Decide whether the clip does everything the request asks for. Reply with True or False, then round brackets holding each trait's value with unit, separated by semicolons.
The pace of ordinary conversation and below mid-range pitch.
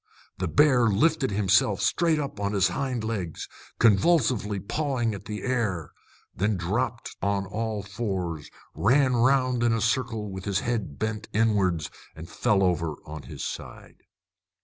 True (150 wpm; 105 Hz)